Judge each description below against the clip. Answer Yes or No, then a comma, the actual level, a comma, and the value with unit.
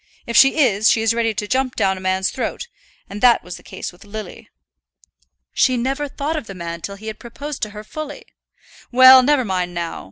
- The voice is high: Yes, high, 225 Hz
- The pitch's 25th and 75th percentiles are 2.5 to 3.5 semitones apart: No, average, 5.1 semitones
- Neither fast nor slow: No, fast, 215 wpm